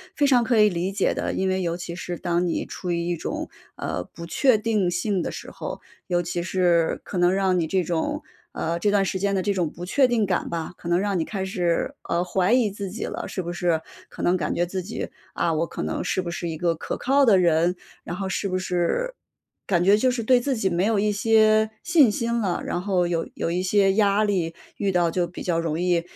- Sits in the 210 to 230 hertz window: No, medium, 185 Hz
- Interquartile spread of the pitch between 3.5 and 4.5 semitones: No, average, 3.1 semitones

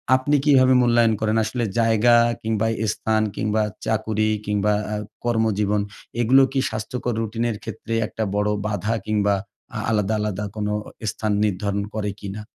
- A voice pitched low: Yes, low, 110 Hz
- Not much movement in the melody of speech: Yes, narrow, 1.7 semitones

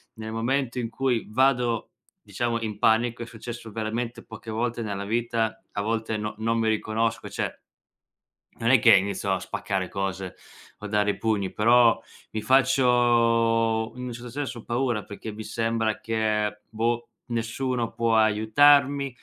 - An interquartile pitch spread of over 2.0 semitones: No, narrow, 1.7 semitones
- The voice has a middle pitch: No, low, 115 Hz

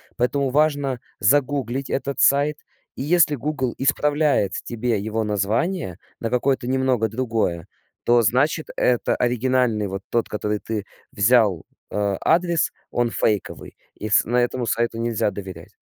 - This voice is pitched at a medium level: No, low, 120 Hz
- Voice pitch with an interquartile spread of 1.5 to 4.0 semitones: No, average, 4.4 semitones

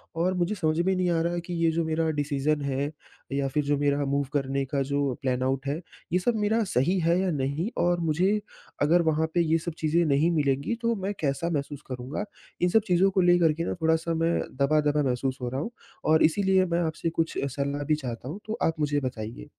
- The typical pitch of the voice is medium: Yes, medium, 155 Hz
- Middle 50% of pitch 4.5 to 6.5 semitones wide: No, average, 3.7 semitones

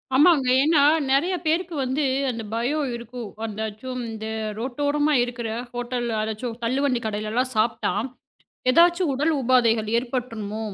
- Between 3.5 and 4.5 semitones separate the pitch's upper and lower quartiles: Yes, average, 4.0 semitones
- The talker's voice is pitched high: Yes, high, 245 Hz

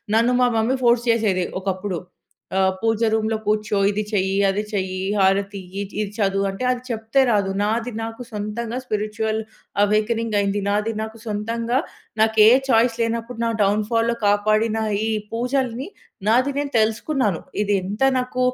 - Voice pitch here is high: Yes, high, 220 Hz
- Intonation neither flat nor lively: No, narrow, 2.2 semitones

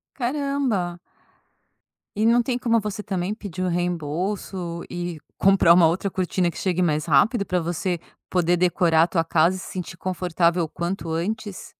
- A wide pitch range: No, average, 2.8 semitones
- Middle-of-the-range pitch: Yes, medium, 180 Hz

